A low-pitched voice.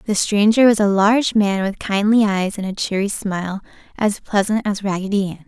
No: high, 205 Hz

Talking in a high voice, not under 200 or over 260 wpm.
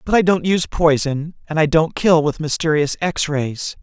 No: medium, 160 Hz; fast, 205 wpm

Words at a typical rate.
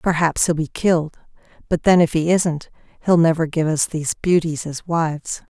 Yes: average, 185 wpm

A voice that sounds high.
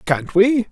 Yes: high, 200 Hz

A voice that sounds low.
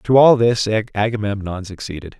Yes: low, 105 Hz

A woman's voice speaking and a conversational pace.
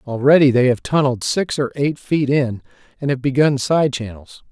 No: male; average, 185 wpm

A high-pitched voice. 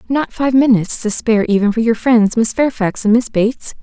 Yes: high, 230 Hz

